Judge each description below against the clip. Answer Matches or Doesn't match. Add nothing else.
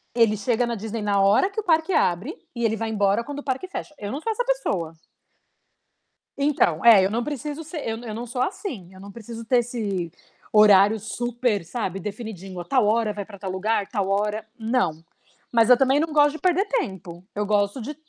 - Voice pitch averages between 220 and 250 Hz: Matches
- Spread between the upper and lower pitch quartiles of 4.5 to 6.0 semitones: Matches